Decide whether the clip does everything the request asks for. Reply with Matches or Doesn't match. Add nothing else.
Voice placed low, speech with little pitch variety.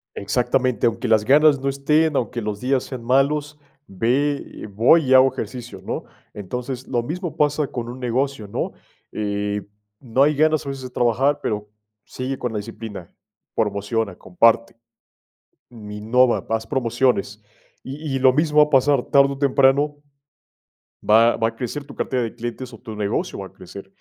Doesn't match